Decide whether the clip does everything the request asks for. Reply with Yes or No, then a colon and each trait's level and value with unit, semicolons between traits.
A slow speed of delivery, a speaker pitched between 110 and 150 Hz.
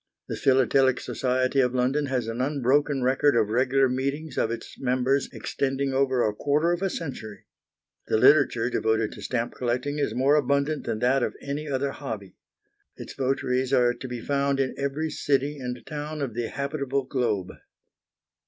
No: average, 170 wpm; low, 135 Hz